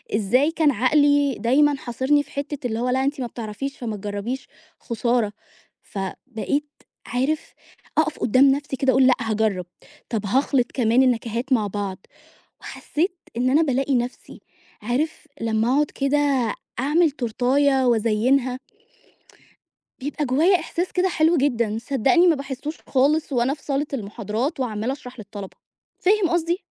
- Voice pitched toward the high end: Yes, very high, 260 Hz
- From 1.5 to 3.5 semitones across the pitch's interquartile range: No, average, 3.9 semitones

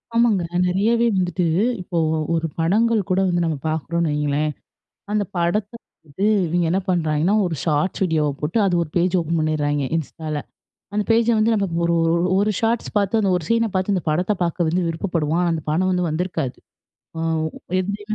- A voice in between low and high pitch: Yes, medium, 175 Hz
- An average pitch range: Yes, average, 4.0 semitones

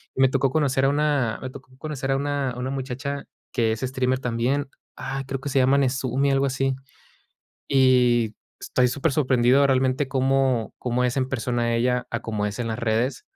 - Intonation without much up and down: Yes, narrow, 1.8 semitones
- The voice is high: No, low, 130 Hz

